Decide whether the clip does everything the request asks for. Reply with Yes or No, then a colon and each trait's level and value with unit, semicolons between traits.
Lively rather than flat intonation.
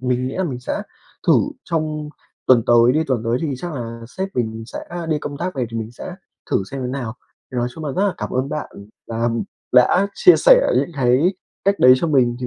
No: average, 4.5 semitones